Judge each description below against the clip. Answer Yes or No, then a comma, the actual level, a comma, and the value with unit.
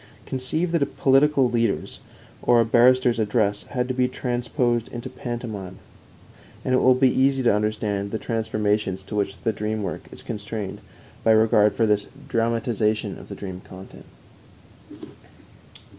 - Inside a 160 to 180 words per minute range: No, average, 150 wpm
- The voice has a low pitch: Yes, low, 115 Hz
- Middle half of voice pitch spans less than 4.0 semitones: Yes, average, 3.1 semitones